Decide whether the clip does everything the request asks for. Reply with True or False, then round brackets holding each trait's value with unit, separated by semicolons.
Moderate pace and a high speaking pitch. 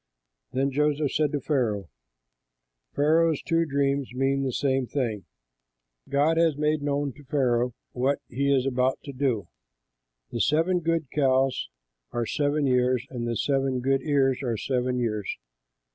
False (145 wpm; 135 Hz)